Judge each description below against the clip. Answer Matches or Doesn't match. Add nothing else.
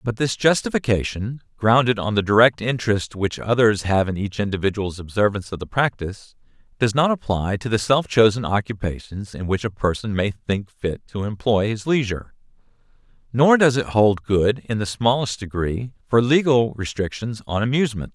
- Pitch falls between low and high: Doesn't match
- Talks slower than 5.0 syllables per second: Doesn't match